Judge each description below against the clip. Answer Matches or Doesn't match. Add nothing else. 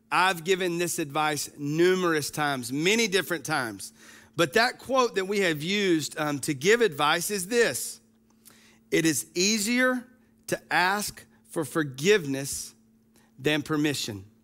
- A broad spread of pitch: Matches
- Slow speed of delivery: Matches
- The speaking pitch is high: Doesn't match